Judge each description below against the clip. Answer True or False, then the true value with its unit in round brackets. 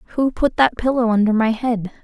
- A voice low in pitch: False (230 Hz)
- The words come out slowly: False (205 wpm)